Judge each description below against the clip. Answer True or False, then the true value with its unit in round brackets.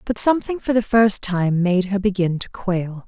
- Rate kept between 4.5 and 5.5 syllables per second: True (4.7 syllables/s)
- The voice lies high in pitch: True (200 Hz)